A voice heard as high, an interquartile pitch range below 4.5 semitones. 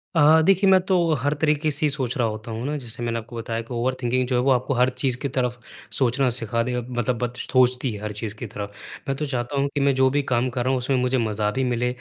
No: low, 125 Hz; narrow, 2.6 semitones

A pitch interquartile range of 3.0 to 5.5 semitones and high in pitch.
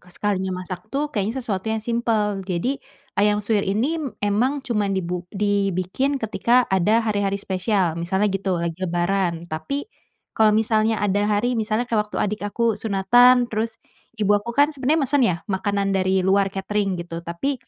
Yes: average, 3.4 semitones; high, 205 Hz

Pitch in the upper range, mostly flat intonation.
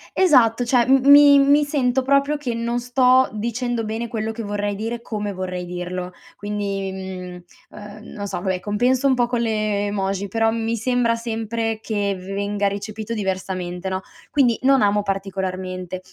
No: high, 215 Hz; average, 3.6 semitones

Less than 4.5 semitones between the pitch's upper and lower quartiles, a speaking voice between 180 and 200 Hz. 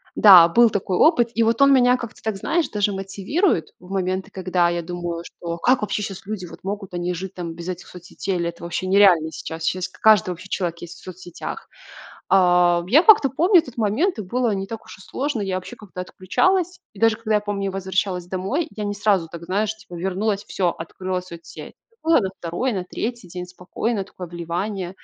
Yes: average, 3.6 semitones; high, 190 Hz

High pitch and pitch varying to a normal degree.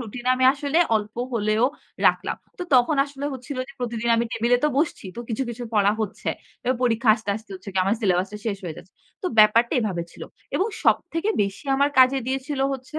Yes: high, 235 Hz; average, 4.1 semitones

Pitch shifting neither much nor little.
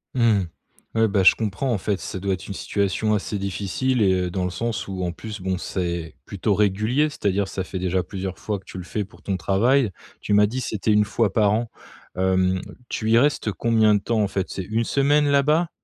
Yes: average, 3.2 semitones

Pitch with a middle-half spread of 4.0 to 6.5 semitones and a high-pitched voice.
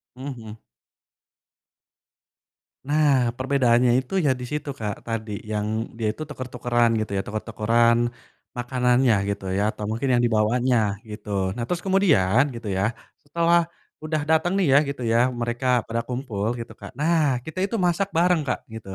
No: average, 4.8 semitones; low, 125 Hz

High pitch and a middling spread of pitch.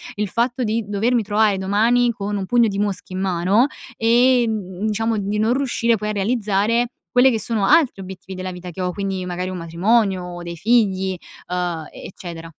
Yes: high, 205 Hz; average, 3.7 semitones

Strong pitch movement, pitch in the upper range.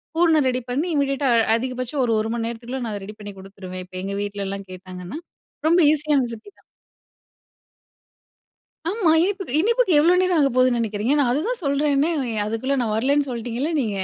Yes: wide, 5.8 semitones; very high, 255 Hz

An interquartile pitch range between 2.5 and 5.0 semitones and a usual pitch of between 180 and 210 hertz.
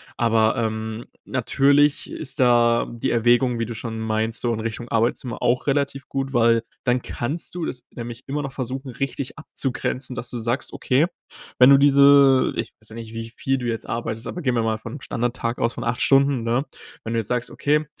No: average, 2.9 semitones; low, 120 Hz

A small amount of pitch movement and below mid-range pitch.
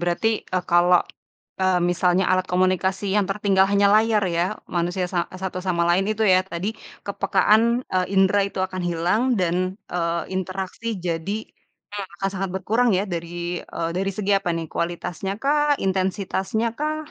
No: narrow, 2.3 semitones; high, 190 Hz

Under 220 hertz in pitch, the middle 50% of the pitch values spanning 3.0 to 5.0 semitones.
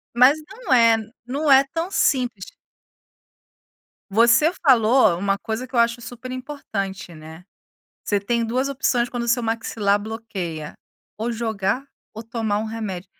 No: high, 230 Hz; average, 3.7 semitones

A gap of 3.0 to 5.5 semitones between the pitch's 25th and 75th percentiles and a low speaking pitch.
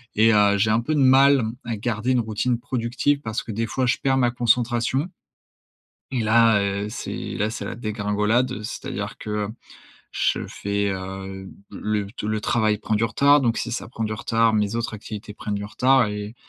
No: narrow, 2.6 semitones; low, 110 Hz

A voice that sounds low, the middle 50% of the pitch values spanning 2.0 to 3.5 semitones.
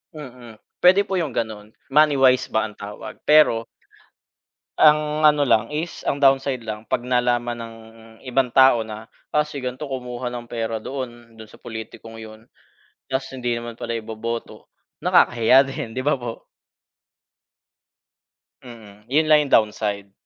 Yes: low, 120 Hz; average, 3.2 semitones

